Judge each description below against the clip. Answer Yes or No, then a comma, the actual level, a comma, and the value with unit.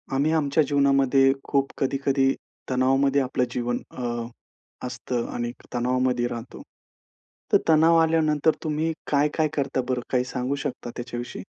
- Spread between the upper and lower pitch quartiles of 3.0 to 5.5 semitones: No, narrow, 2.6 semitones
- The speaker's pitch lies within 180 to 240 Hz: No, low, 135 Hz